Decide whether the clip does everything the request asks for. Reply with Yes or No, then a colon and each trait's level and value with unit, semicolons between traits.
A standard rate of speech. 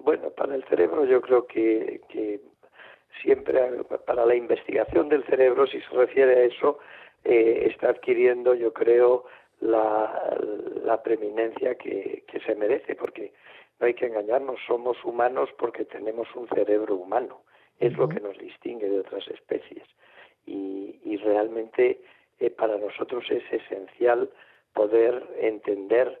Yes: average, 140 wpm